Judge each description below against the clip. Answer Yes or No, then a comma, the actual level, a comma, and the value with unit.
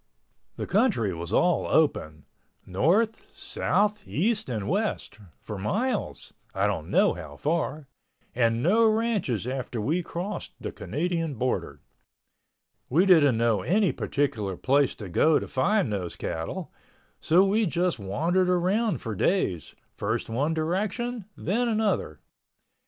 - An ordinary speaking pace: No, slow, 125 wpm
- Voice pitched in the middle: Yes, medium, 160 Hz